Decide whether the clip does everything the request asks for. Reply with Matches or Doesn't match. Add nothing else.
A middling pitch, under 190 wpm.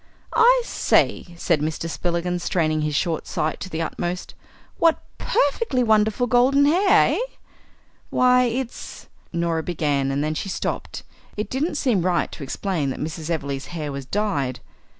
Matches